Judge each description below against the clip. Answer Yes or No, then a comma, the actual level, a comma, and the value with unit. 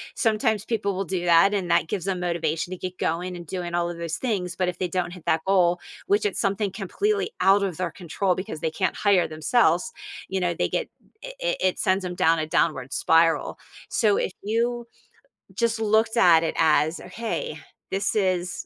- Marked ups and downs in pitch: No, average, 3.2 semitones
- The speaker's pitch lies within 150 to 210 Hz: Yes, medium, 185 Hz